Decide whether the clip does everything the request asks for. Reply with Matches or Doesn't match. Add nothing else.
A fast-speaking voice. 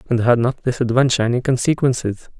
Doesn't match